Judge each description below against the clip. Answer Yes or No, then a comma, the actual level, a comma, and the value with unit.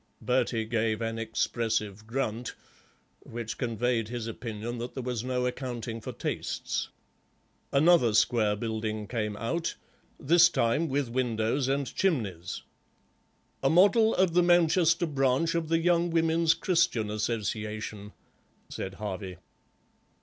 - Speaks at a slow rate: Yes, slow, 120 wpm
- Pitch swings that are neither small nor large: No, wide, 6.6 semitones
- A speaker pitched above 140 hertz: No, low, 120 Hz